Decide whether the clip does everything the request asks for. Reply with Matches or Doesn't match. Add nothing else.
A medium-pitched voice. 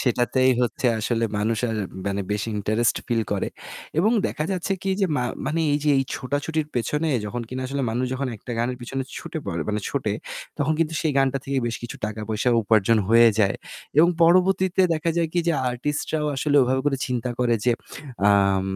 Doesn't match